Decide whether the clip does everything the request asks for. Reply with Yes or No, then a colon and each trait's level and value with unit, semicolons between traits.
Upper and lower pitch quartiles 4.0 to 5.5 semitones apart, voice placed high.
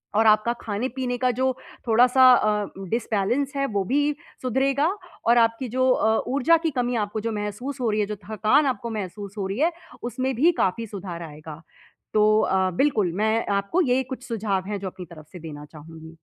Yes: average, 4.6 semitones; high, 220 Hz